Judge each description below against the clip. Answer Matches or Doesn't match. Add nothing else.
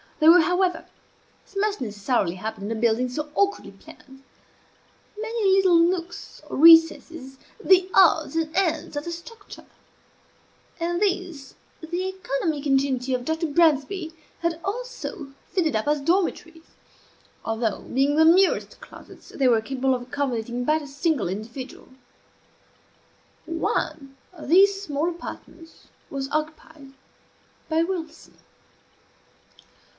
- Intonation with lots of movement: Doesn't match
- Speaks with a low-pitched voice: Doesn't match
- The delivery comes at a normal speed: Doesn't match